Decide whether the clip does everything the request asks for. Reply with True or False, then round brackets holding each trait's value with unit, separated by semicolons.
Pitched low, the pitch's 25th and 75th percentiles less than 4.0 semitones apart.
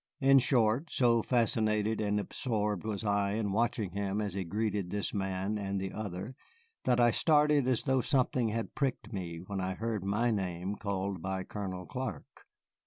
True (105 Hz; 3.4 semitones)